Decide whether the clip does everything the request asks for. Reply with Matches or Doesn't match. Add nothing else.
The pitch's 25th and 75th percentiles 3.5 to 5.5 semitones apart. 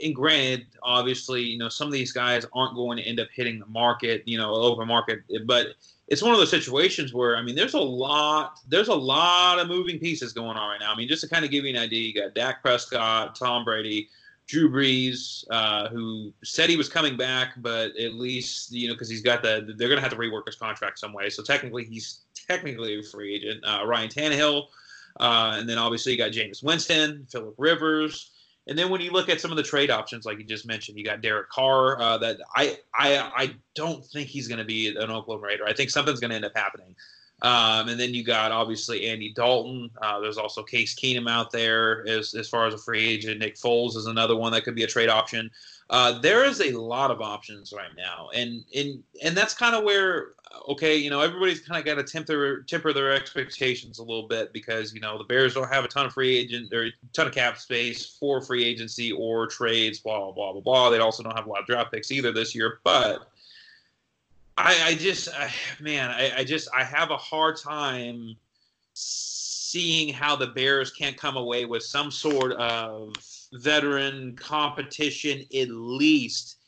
Matches